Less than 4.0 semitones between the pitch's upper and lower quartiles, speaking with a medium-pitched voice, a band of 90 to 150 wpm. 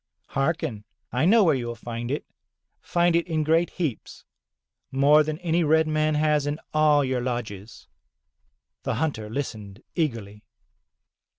No: average, 4.9 semitones; medium, 145 Hz; average, 140 wpm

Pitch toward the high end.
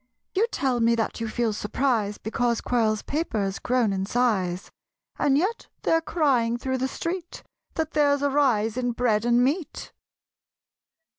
Yes: high, 245 Hz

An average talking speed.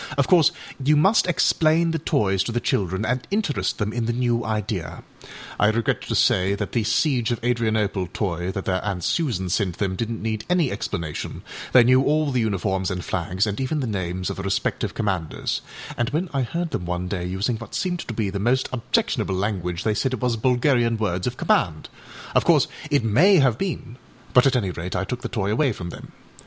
No: fast, 210 wpm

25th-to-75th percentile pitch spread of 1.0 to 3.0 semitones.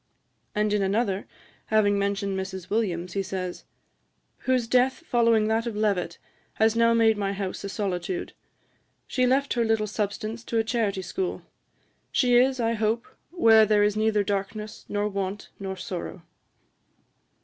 Yes: narrow, 2.6 semitones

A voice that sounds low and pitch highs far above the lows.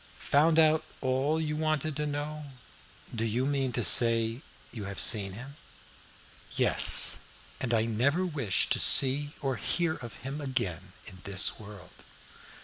No: low, 130 Hz; average, 5.0 semitones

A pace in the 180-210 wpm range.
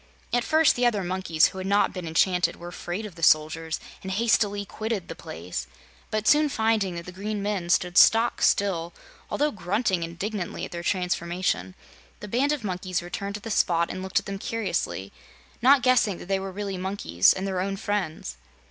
Yes: average, 190 wpm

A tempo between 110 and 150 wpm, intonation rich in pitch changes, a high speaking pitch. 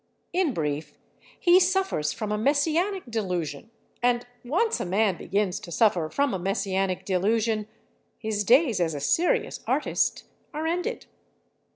Yes: slow, 135 wpm; wide, 9.0 semitones; high, 220 Hz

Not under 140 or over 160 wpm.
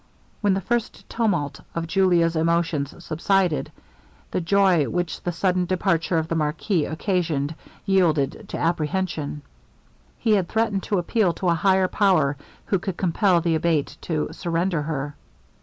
Yes: average, 145 wpm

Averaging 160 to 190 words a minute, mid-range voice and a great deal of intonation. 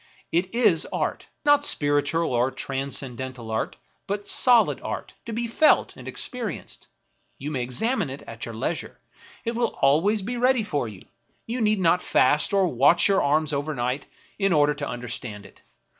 Yes: average, 170 wpm; medium, 155 Hz; wide, 8.3 semitones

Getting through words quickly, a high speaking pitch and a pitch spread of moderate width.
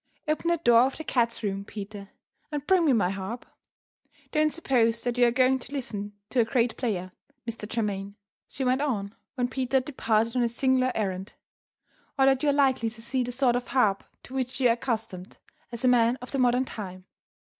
Yes: fast, 210 wpm; high, 245 Hz; average, 3.3 semitones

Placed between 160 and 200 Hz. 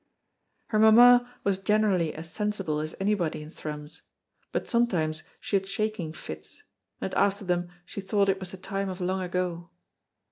Yes: high, 190 Hz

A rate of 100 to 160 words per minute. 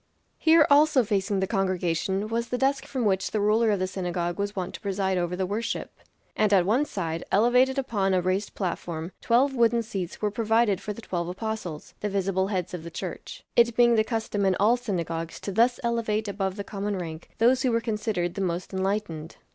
No: fast, 205 wpm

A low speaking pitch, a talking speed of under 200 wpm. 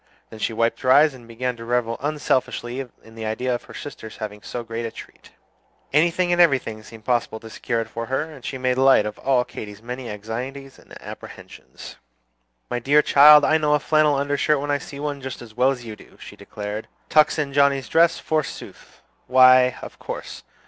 No: low, 130 Hz; fast, 205 wpm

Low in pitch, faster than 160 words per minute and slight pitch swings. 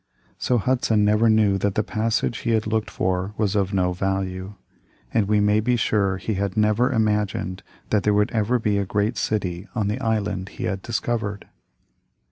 Yes: low, 105 Hz; average, 185 wpm; narrow, 2.0 semitones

